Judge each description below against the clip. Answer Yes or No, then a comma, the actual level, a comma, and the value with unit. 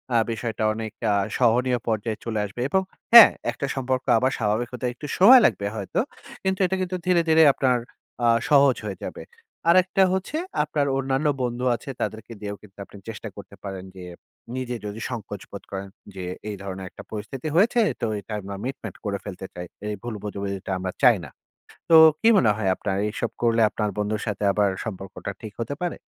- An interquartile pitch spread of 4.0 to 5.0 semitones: Yes, average, 4.6 semitones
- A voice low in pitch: Yes, low, 115 Hz